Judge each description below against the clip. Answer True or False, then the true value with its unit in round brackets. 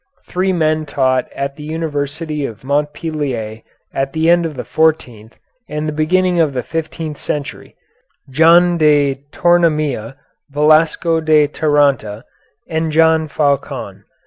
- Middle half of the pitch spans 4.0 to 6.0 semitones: False (2.5 semitones)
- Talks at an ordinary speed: False (125 wpm)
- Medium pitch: True (150 Hz)